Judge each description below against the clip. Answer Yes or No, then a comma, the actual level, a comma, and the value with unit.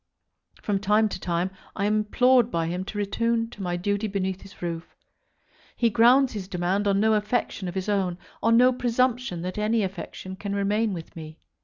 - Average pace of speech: Yes, average, 190 wpm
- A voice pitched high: Yes, high, 205 Hz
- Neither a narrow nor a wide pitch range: Yes, average, 3.5 semitones